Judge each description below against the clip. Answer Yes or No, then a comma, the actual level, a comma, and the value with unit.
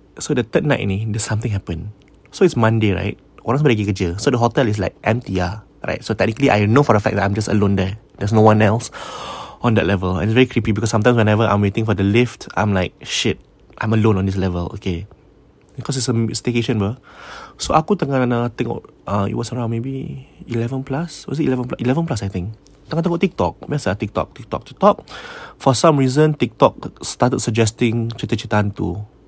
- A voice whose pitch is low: Yes, low, 115 Hz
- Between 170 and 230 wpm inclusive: Yes, average, 200 wpm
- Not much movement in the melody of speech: No, average, 4.0 semitones